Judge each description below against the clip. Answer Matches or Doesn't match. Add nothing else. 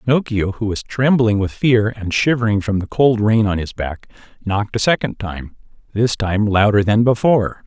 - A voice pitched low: Matches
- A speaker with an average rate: Matches